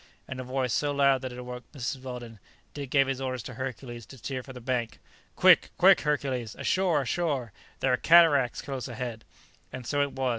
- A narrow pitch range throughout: Yes, narrow, 2.0 semitones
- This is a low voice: Yes, low, 130 Hz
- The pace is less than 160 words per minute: No, average, 200 wpm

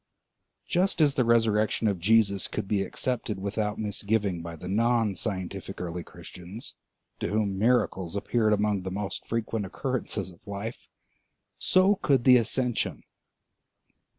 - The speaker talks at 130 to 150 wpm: Yes, slow, 135 wpm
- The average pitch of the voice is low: Yes, low, 105 Hz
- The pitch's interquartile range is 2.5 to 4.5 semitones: Yes, average, 3.2 semitones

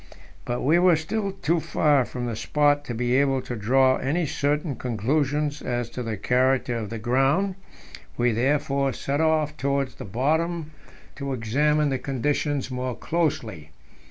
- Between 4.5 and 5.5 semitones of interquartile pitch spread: No, average, 3.6 semitones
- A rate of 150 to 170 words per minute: Yes, average, 155 wpm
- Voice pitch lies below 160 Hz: Yes, medium, 140 Hz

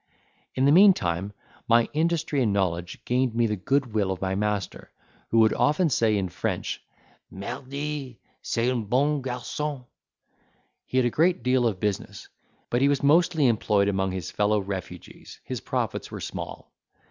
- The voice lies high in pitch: No, low, 120 Hz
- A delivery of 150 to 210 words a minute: Yes, average, 160 wpm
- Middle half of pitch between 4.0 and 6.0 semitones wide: Yes, wide, 5.6 semitones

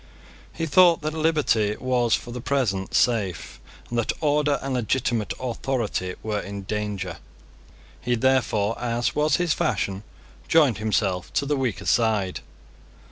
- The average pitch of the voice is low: Yes, low, 120 Hz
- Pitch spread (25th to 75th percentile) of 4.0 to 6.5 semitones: Yes, average, 5.2 semitones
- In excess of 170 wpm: No, slow, 135 wpm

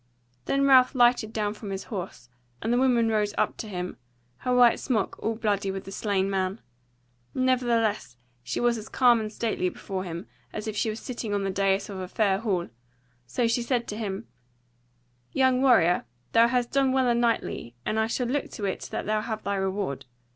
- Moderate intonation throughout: Yes, average, 3.7 semitones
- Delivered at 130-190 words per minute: No, average, 200 wpm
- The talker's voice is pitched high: Yes, high, 215 Hz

